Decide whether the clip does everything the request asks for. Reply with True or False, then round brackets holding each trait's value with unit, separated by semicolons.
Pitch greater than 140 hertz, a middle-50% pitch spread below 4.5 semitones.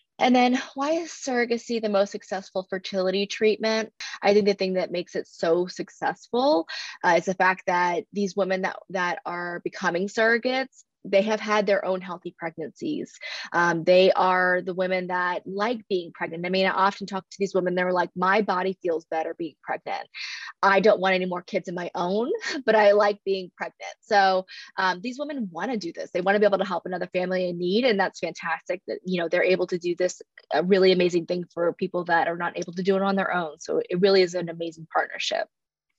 True (190 Hz; 2.9 semitones)